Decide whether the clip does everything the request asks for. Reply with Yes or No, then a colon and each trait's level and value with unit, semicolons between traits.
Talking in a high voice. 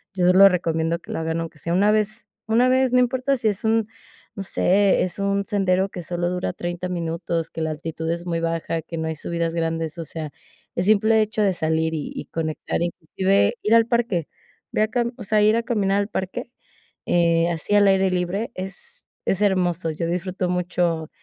No: medium, 180 Hz